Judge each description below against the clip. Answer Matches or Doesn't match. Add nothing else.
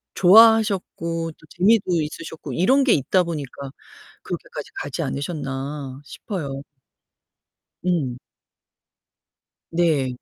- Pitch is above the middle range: Doesn't match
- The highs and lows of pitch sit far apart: Doesn't match